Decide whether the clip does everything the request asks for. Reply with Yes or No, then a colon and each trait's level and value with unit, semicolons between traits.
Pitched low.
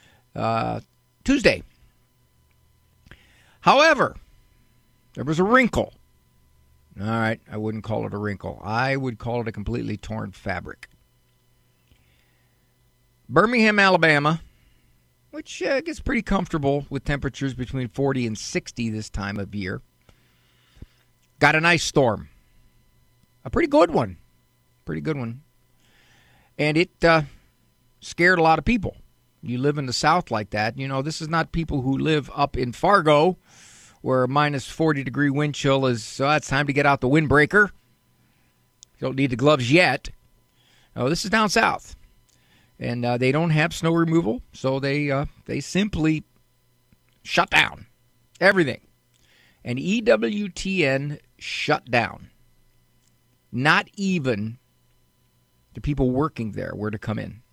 Yes: low, 130 Hz